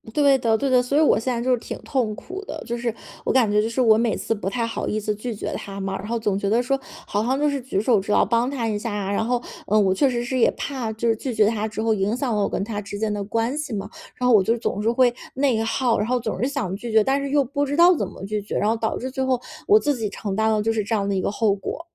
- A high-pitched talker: Yes, high, 225 Hz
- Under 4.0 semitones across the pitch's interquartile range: Yes, average, 3.5 semitones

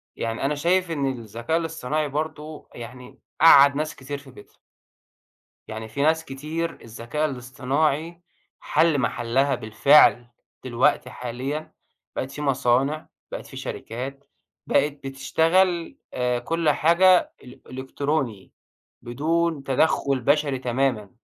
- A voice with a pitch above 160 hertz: No, medium, 140 Hz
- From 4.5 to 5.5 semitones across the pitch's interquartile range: No, average, 3.8 semitones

